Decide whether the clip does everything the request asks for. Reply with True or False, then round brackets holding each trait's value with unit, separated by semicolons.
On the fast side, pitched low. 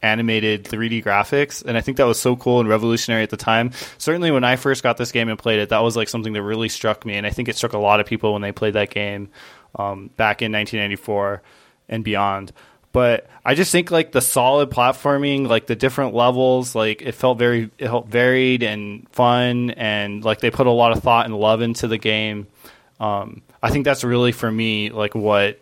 True (225 wpm; 115 Hz)